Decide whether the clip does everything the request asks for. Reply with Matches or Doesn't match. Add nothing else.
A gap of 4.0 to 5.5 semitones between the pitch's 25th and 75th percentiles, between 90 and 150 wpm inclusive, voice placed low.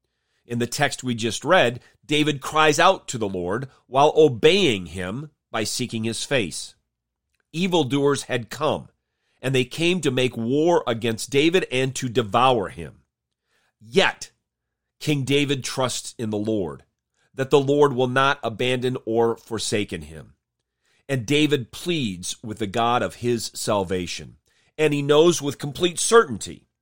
Matches